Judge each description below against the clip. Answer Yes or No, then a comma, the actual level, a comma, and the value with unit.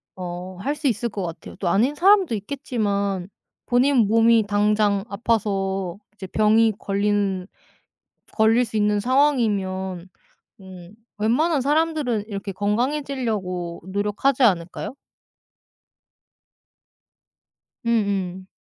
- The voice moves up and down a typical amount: Yes, average, 4.2 semitones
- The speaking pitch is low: No, high, 210 Hz